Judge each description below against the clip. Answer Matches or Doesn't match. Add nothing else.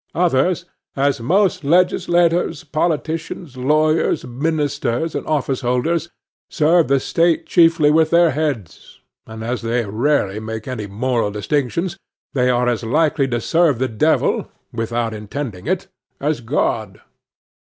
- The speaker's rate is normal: Doesn't match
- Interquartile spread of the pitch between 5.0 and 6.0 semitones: Matches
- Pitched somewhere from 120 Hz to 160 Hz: Matches